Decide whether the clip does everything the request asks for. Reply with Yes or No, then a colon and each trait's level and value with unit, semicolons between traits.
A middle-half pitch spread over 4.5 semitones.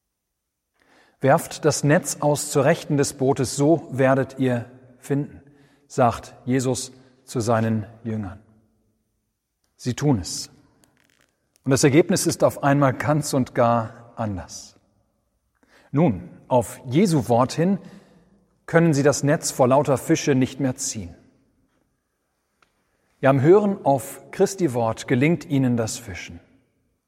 No: average, 3.9 semitones